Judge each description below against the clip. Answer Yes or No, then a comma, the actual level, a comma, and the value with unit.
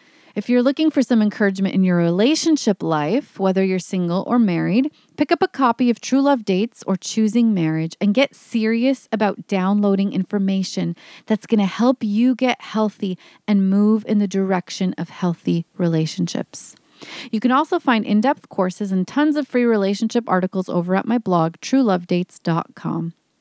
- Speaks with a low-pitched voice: No, high, 210 Hz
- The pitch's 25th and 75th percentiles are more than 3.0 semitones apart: Yes, average, 4.7 semitones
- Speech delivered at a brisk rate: No, average, 165 wpm